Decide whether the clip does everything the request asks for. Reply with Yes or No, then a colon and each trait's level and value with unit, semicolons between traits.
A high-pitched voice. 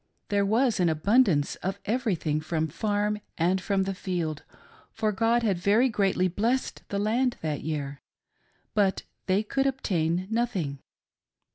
Yes: high, 195 Hz